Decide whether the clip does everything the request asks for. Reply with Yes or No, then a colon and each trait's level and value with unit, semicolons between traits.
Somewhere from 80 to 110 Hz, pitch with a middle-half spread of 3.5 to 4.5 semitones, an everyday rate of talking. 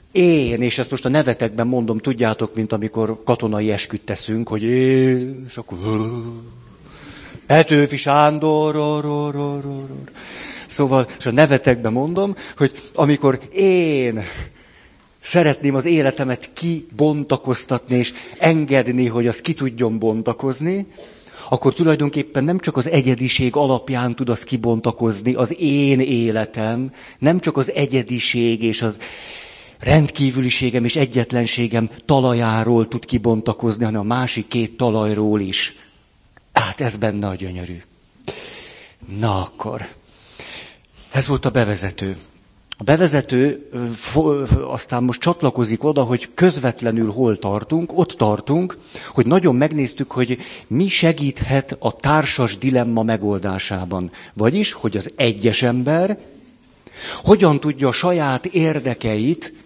No: low, 125 Hz; average, 3.9 semitones; average, 120 wpm